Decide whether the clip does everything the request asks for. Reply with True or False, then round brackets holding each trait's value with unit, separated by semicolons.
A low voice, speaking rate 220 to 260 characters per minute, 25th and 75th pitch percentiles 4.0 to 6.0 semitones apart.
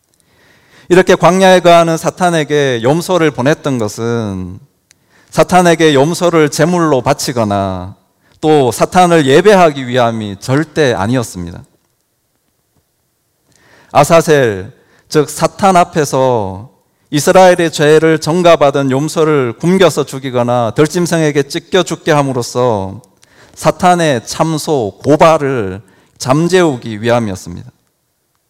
False (145 Hz; 245 characters per minute; 5.5 semitones)